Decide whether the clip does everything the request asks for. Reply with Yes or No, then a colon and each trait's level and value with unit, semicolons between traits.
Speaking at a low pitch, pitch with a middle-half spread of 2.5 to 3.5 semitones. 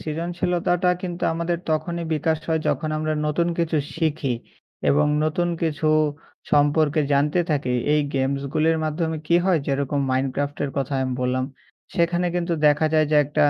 No: medium, 155 Hz; average, 2.8 semitones